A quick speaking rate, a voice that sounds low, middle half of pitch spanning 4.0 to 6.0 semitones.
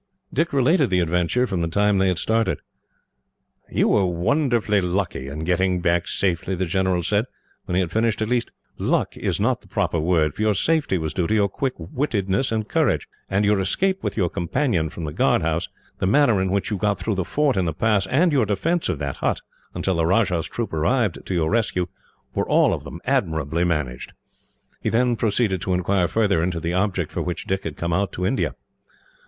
Yes: fast, 210 wpm; very low, 95 Hz; average, 4.4 semitones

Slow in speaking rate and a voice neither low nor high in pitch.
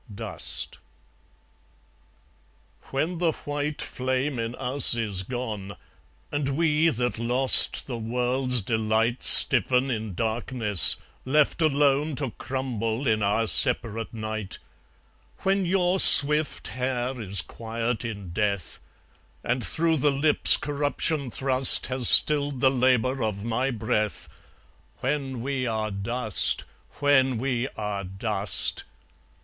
No: slow, 115 wpm; low, 125 Hz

